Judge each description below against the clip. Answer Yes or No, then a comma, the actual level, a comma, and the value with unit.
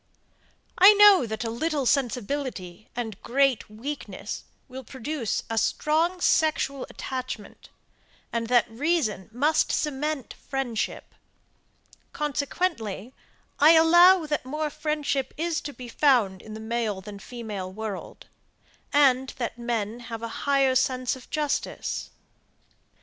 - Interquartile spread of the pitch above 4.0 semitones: Yes, average, 4.9 semitones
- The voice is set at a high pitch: Yes, very high, 260 Hz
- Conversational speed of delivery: No, slow, 120 wpm